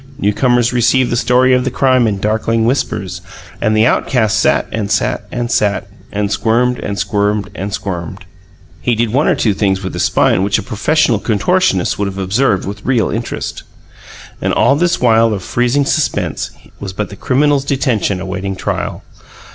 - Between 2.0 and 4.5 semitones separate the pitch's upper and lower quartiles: Yes, average, 3.9 semitones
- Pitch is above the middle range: No, low, 110 Hz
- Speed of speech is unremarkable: Yes, average, 175 wpm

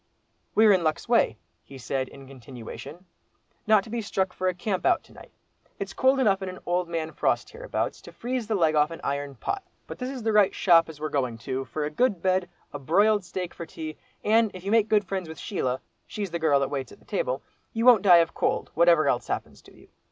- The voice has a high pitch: No, medium, 180 Hz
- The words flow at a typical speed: No, fast, 235 wpm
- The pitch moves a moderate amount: No, wide, 6.3 semitones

